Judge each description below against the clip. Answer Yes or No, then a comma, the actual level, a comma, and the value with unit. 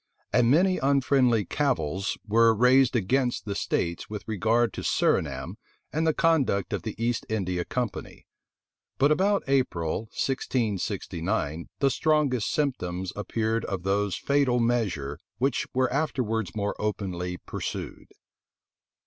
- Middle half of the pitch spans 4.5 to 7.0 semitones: Yes, wide, 5.5 semitones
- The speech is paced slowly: Yes, slow, 125 wpm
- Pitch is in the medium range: No, low, 115 Hz